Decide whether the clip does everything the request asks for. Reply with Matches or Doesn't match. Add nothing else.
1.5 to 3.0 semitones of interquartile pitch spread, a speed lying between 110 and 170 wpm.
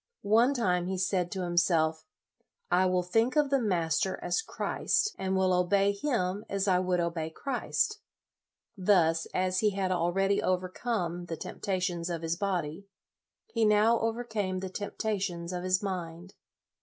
Matches